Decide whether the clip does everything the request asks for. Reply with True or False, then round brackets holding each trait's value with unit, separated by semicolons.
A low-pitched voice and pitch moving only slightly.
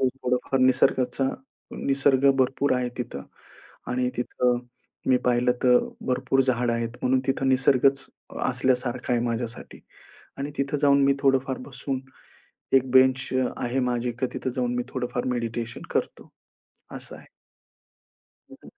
True (130 Hz; 1.5 semitones)